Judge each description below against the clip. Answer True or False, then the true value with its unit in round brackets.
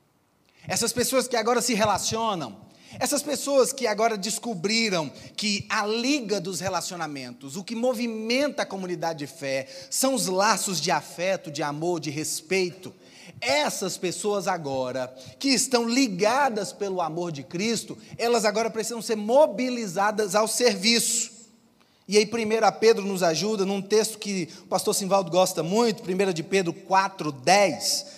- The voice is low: False (205 Hz)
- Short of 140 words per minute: False (145 wpm)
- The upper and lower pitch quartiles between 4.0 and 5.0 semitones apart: True (4.5 semitones)